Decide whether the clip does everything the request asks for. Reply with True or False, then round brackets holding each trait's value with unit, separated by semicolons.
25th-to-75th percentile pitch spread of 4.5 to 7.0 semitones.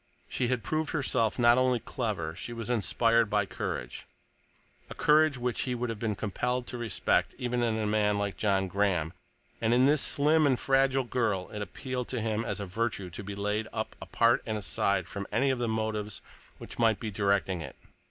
False (3.4 semitones)